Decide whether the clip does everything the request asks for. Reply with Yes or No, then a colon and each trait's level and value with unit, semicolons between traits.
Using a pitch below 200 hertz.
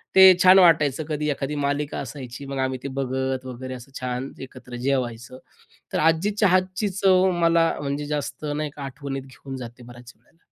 Yes: medium, 140 Hz